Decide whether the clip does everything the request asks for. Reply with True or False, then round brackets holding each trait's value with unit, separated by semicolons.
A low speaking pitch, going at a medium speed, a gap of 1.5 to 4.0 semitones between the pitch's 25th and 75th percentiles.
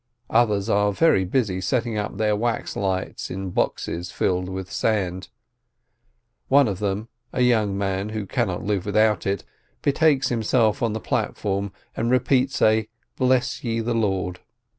True (105 Hz; 150 wpm; 3.4 semitones)